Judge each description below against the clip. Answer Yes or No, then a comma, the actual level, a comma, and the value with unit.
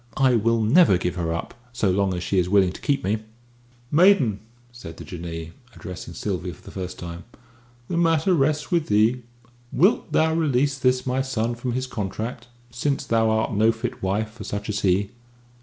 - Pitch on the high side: No, low, 115 Hz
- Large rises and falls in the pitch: Yes, wide, 5.8 semitones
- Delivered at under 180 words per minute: No, average, 190 wpm